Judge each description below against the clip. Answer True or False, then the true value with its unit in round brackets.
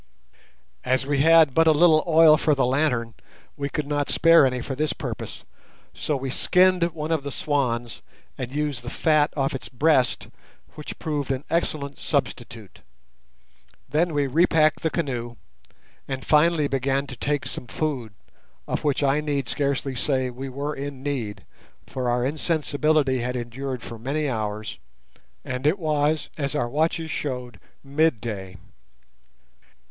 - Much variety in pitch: False (3.2 semitones)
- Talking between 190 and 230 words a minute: False (150 wpm)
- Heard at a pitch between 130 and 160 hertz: True (140 Hz)